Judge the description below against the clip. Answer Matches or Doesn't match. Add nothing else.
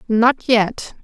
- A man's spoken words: Doesn't match